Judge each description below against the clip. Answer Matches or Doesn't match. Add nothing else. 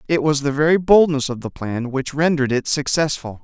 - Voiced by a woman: Doesn't match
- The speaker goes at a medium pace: Doesn't match